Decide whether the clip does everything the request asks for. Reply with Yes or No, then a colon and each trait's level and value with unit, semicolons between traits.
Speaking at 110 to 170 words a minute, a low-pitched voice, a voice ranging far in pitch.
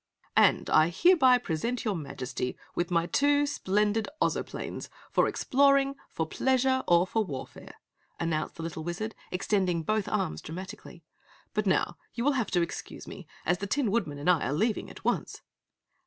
No: average, 165 wpm; high, 190 Hz; wide, 6.6 semitones